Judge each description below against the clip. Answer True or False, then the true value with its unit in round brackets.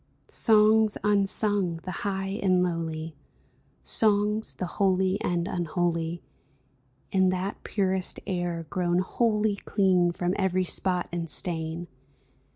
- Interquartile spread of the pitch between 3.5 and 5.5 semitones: False (2.5 semitones)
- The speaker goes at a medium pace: False (110 wpm)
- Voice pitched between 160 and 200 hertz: True (185 Hz)